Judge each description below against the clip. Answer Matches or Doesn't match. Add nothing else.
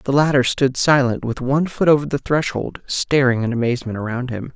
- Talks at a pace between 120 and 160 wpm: Doesn't match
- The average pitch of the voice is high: Doesn't match